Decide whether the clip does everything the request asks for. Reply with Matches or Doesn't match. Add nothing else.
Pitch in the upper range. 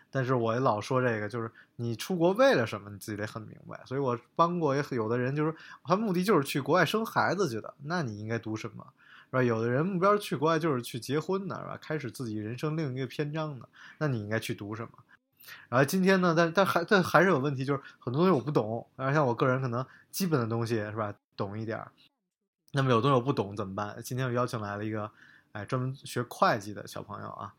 Doesn't match